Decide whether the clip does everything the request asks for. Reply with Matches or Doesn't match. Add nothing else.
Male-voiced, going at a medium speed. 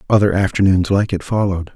Matches